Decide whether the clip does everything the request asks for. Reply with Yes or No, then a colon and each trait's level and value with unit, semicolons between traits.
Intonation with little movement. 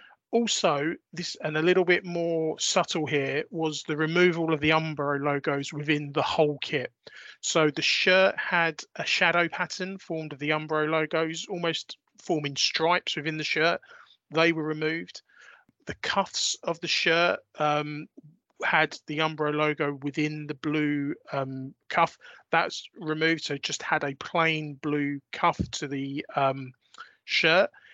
Yes: narrow, 2.2 semitones